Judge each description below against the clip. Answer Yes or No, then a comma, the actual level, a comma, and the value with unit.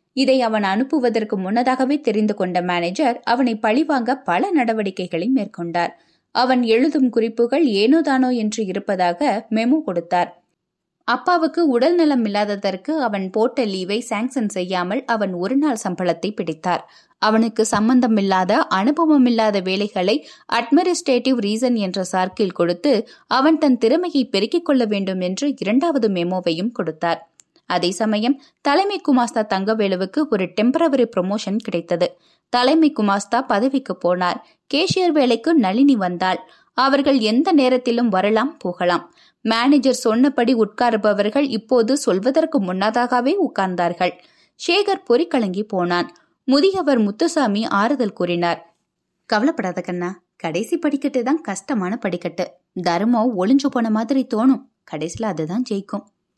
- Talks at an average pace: Yes, average, 110 wpm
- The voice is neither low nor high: No, high, 225 Hz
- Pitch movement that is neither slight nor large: No, wide, 6.1 semitones